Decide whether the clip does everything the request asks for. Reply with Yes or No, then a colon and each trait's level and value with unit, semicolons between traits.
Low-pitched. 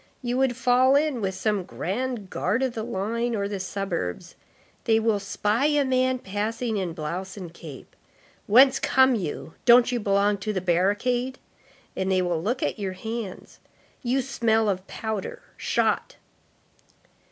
No: high, 215 Hz